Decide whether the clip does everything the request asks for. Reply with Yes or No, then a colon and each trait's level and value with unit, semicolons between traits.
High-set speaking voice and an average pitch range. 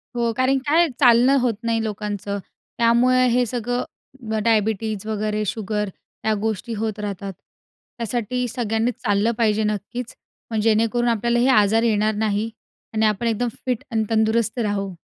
No: high, 225 Hz; narrow, 2.1 semitones